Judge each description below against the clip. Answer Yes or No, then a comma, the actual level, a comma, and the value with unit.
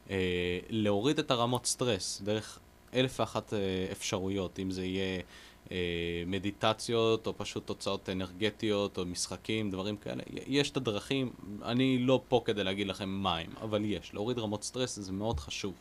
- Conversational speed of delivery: No, fast, 160 wpm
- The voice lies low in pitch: Yes, low, 100 Hz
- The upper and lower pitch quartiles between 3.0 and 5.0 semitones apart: Yes, average, 3.3 semitones